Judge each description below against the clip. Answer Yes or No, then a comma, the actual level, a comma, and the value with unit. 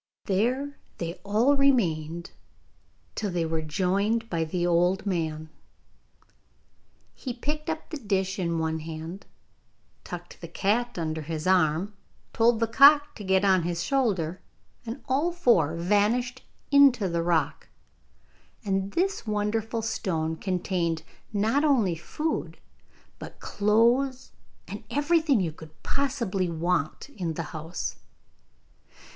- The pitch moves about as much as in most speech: No, wide, 6.4 semitones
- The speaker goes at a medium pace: No, slow, 125 wpm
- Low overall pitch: No, high, 195 Hz